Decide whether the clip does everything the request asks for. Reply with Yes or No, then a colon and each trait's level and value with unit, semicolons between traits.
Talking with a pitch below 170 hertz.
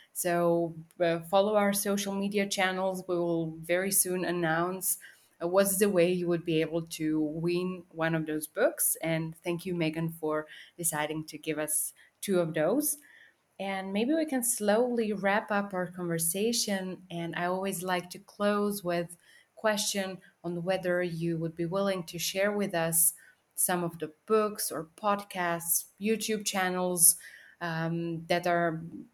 No: medium, 175 Hz